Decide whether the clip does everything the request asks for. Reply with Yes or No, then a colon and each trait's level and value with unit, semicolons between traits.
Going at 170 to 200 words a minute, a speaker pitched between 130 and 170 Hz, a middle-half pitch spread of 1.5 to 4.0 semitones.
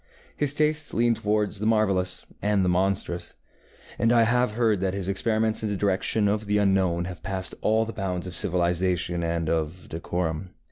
No: average, 180 wpm; very low, 95 Hz; average, 3.4 semitones